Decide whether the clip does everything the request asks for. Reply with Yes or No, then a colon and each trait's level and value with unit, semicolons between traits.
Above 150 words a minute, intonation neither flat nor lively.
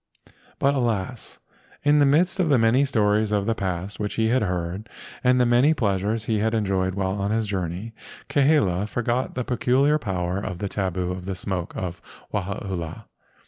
Yes: average, 180 wpm; average, 4.8 semitones